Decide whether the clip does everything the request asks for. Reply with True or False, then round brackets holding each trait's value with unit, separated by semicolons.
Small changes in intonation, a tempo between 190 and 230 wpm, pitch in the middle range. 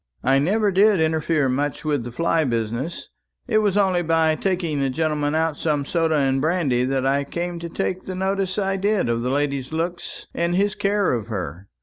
False (5.2 semitones; 200 wpm; 160 Hz)